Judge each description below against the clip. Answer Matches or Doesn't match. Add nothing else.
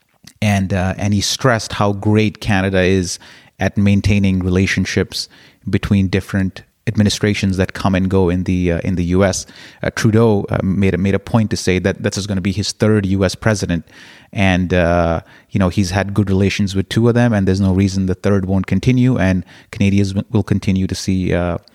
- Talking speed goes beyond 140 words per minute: Matches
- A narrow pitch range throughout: Matches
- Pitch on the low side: Matches